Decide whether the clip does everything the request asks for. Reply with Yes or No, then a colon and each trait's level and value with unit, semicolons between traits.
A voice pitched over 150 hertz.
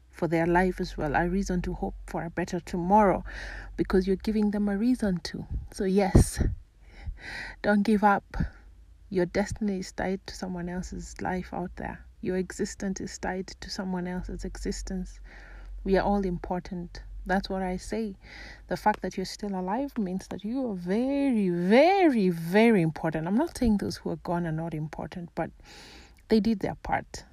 Yes: high, 190 Hz